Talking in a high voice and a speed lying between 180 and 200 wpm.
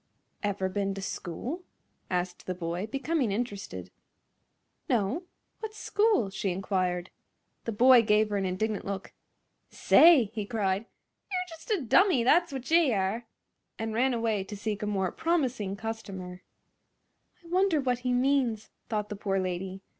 No: high, 215 Hz; average, 150 wpm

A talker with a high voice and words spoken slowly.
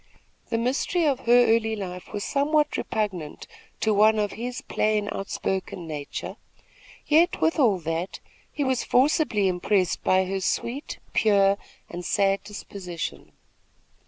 Yes: high, 210 Hz; slow, 130 wpm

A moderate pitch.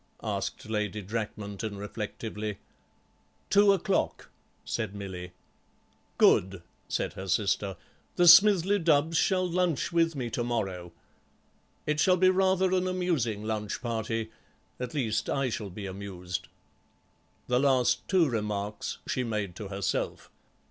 No: low, 115 Hz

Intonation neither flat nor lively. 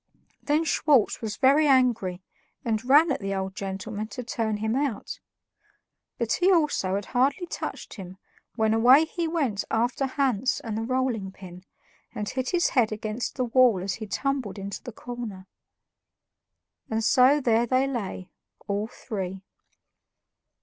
Yes: average, 4.4 semitones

